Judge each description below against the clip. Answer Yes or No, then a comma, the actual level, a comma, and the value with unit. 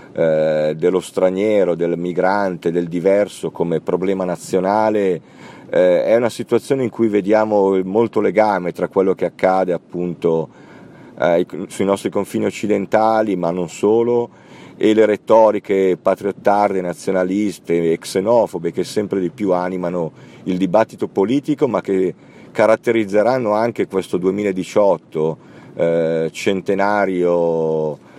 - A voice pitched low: Yes, very low, 95 Hz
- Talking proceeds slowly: Yes, slow, 110 wpm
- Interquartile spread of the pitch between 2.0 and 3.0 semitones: No, average, 3.5 semitones